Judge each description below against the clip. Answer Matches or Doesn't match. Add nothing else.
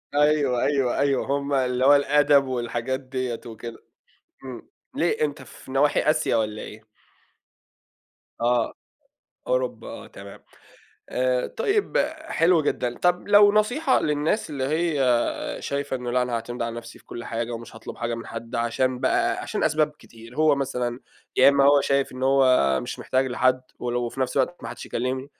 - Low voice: Matches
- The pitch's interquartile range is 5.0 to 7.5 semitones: Doesn't match